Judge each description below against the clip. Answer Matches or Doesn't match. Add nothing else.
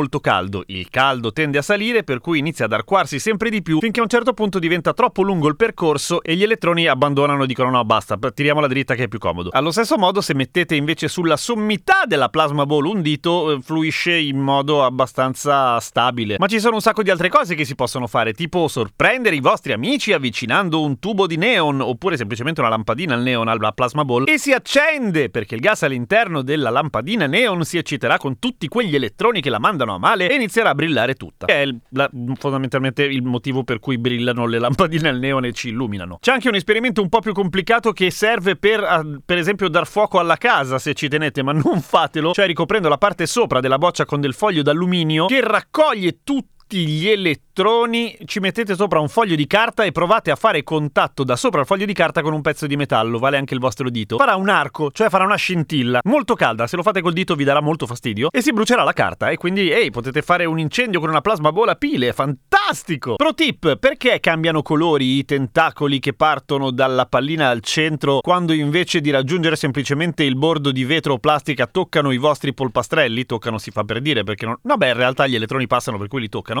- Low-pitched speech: Doesn't match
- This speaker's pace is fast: Matches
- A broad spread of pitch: Matches